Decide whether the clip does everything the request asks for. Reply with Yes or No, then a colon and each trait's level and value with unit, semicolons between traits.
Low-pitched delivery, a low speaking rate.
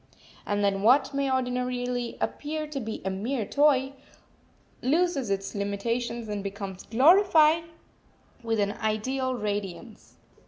No: high, 245 Hz; slow, 120 wpm